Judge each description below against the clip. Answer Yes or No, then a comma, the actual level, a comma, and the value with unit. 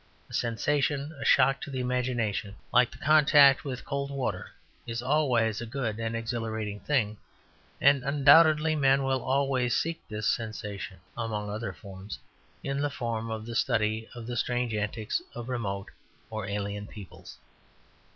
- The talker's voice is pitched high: No, low, 120 Hz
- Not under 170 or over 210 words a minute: No, average, 150 wpm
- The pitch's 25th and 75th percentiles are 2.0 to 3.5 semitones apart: No, average, 4.0 semitones